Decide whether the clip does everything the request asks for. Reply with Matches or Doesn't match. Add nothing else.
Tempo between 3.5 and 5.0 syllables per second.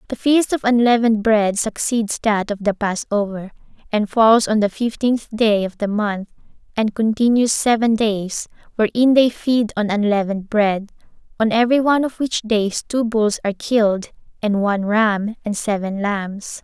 Matches